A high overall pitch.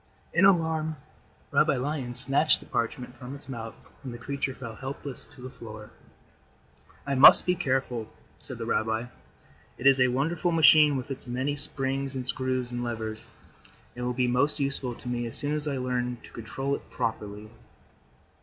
No: low, 130 Hz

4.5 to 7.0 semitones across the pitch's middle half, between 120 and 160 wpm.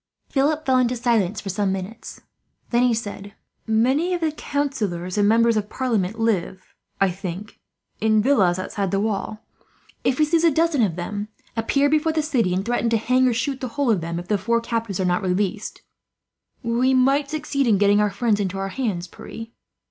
No: average, 4.8 semitones; average, 195 wpm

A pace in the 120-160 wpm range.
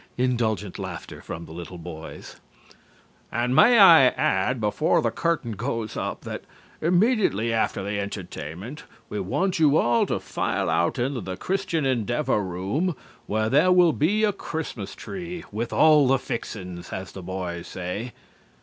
Yes: average, 150 wpm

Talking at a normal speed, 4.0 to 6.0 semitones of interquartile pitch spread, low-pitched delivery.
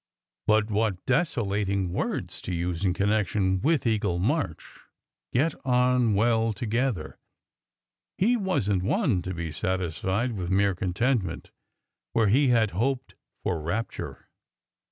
No: slow, 130 wpm; average, 4.9 semitones; low, 105 Hz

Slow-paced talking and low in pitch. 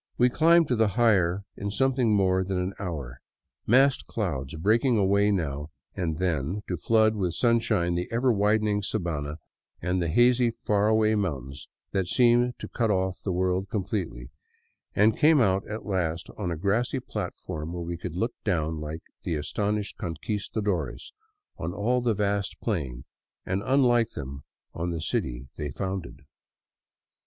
No: average, 155 wpm; low, 100 Hz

